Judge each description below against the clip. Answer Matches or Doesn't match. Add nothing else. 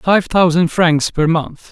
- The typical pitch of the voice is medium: Matches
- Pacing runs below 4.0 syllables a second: Matches